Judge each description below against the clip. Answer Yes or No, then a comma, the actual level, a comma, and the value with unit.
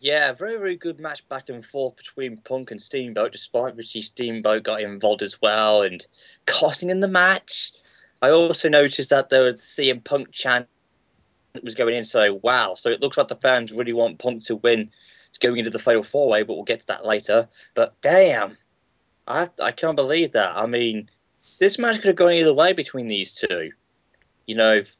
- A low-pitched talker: Yes, low, 125 Hz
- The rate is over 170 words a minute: Yes, average, 200 wpm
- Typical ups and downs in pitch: Yes, average, 4.3 semitones